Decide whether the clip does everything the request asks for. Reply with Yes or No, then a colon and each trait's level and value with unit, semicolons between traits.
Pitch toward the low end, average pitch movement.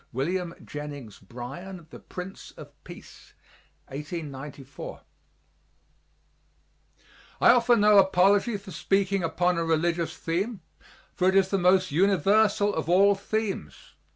No: medium, 180 Hz; average, 3.7 semitones